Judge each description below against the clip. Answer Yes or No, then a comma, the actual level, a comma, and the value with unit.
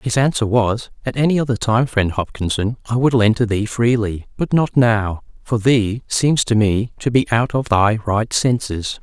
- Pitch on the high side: No, low, 115 Hz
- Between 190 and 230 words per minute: Yes, average, 200 wpm